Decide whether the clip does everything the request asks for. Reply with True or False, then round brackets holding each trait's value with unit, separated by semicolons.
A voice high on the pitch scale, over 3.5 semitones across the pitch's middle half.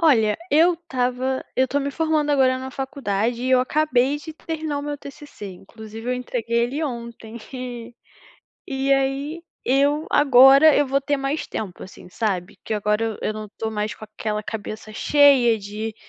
True (255 Hz; 4.4 semitones)